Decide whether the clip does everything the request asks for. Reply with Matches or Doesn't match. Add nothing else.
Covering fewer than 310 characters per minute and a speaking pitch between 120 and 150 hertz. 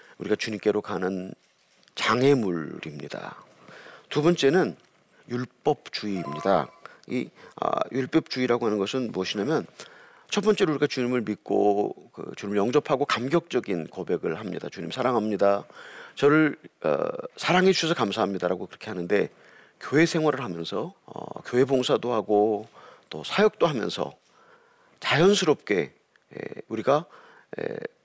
Matches